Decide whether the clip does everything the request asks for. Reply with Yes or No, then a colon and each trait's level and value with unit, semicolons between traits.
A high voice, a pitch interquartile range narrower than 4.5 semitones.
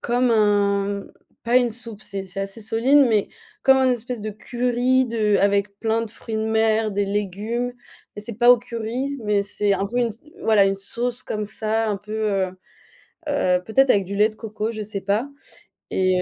Yes: high, 220 Hz; average, 2.8 semitones